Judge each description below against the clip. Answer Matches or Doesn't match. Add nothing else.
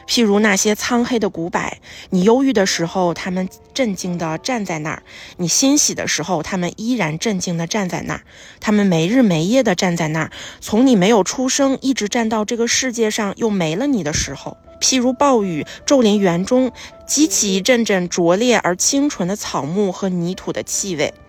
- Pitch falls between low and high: Doesn't match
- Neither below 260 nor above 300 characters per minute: Matches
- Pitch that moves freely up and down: Matches